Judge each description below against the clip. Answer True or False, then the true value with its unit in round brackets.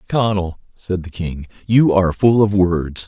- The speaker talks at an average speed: True (175 wpm)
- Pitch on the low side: True (95 Hz)